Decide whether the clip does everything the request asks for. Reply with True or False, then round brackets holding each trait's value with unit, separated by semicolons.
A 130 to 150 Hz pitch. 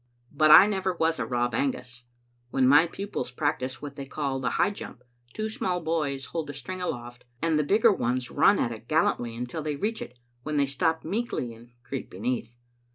True (140 Hz)